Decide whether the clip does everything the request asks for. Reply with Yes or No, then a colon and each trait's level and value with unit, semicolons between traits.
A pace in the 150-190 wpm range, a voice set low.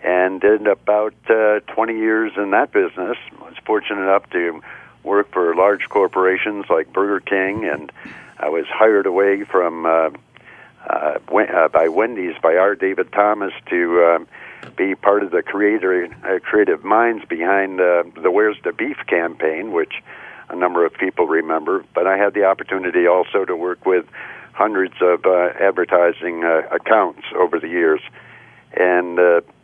Yes: average, 160 wpm; very low, 95 Hz